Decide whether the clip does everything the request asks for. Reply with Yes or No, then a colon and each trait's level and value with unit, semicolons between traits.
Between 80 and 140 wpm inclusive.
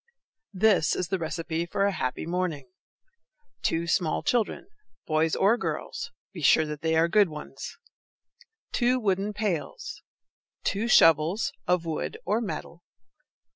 Yes: slow, 135 wpm